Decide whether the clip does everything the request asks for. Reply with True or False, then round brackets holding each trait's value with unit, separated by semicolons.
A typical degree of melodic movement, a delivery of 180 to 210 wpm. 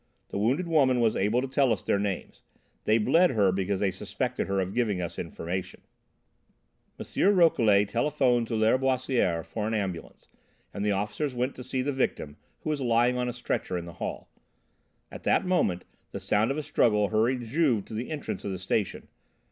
True (4.6 semitones; 190 wpm)